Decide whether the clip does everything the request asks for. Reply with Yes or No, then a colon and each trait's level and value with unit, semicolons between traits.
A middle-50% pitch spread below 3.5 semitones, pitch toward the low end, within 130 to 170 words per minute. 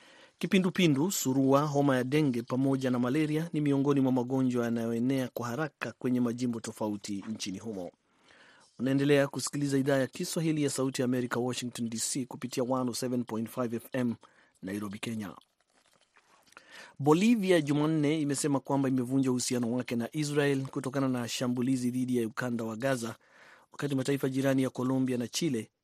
Yes: narrow, 2.6 semitones; low, 130 Hz; average, 135 wpm